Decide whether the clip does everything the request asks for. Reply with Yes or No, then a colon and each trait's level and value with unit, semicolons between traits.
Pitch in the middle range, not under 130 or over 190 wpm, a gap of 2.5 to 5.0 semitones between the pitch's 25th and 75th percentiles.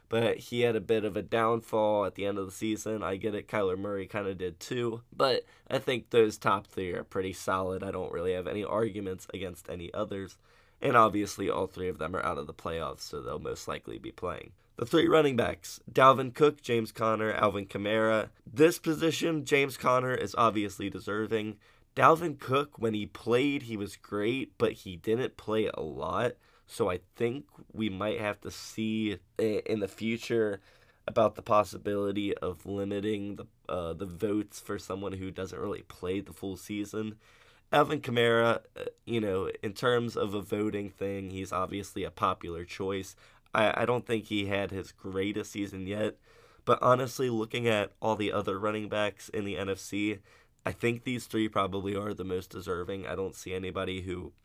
No: low, 105 Hz; average, 185 wpm; average, 3.2 semitones